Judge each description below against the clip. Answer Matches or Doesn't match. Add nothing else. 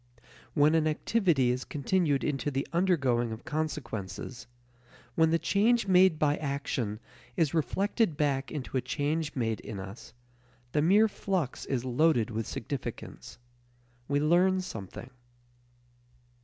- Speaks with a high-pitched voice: Doesn't match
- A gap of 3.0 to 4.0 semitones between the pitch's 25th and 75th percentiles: Doesn't match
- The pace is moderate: Doesn't match